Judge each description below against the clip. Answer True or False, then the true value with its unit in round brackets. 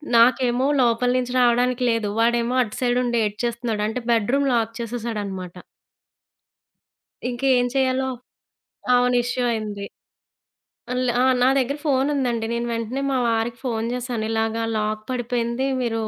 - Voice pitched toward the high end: True (240 Hz)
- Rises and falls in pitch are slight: True (1.8 semitones)